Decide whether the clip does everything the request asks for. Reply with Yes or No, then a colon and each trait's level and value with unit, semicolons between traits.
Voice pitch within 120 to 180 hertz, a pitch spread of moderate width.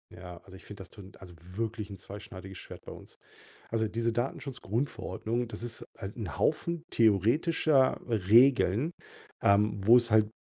No: low, 110 Hz; average, 3.4 semitones